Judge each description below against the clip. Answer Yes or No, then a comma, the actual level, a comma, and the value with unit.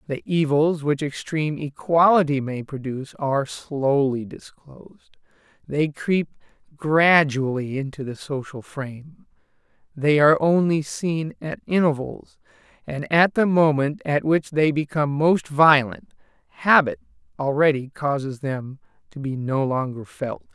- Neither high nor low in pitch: Yes, medium, 145 Hz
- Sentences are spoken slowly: Yes, slow, 125 wpm